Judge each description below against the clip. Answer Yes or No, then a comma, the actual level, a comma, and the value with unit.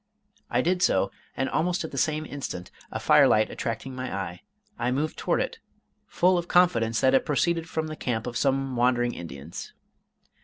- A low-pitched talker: Yes, low, 130 Hz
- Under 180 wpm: No, average, 185 wpm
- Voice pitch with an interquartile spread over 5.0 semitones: Yes, wide, 5.5 semitones